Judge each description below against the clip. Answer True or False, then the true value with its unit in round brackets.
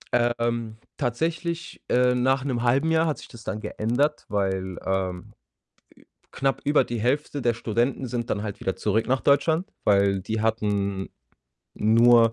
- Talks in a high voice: False (120 Hz)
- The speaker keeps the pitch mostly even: False (4.2 semitones)